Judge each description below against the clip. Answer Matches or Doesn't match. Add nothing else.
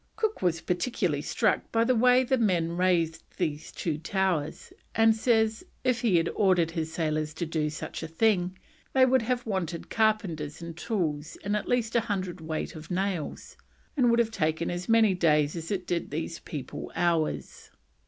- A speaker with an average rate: Matches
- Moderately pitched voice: Matches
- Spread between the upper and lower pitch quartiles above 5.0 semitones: Matches